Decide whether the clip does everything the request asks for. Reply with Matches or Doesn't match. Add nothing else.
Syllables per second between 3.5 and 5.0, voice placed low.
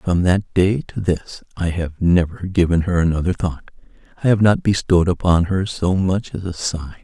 Matches